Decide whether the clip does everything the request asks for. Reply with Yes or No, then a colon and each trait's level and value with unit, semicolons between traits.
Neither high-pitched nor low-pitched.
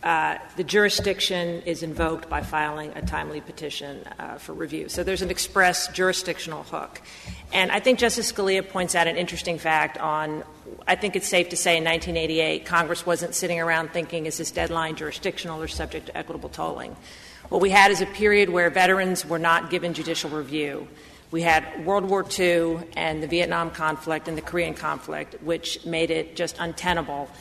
Yes: medium, 170 Hz